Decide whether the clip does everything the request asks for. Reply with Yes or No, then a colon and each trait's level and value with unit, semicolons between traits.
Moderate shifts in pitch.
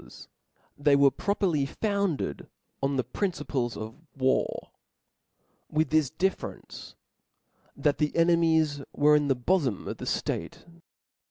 Yes: average, 3.5 semitones